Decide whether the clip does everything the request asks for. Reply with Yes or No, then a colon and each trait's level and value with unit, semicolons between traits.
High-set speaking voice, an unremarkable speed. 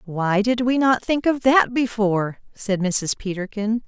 Yes: high, 220 Hz; average, 170 wpm